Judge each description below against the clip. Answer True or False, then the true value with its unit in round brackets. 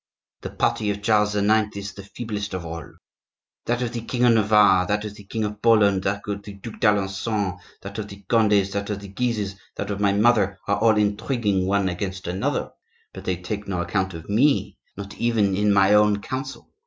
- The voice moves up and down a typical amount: False (1.6 semitones)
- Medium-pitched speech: False (105 Hz)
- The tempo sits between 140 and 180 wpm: False (205 wpm)